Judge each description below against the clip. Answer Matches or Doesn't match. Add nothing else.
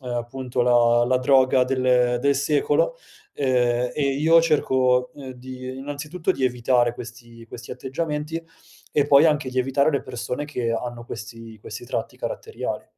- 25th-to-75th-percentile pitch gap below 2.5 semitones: Doesn't match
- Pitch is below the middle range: Matches